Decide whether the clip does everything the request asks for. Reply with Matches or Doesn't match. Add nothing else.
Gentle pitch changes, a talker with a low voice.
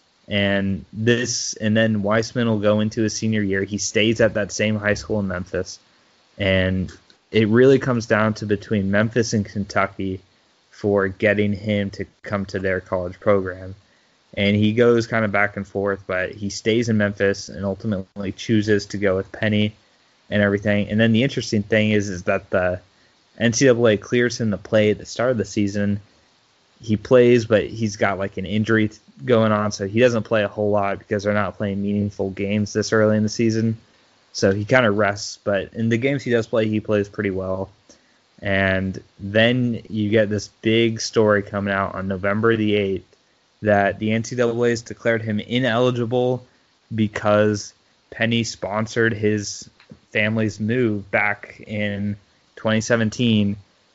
Matches